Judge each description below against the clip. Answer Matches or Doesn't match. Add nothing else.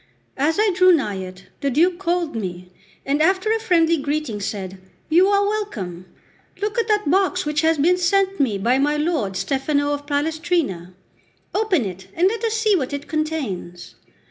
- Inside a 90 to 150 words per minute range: Doesn't match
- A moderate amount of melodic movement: Doesn't match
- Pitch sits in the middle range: Doesn't match